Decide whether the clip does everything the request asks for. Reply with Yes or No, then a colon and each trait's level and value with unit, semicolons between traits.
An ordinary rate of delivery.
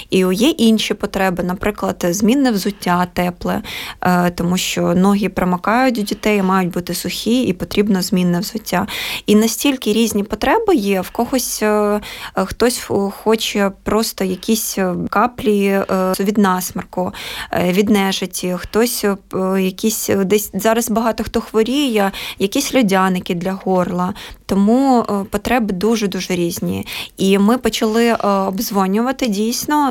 Yes: average, 115 wpm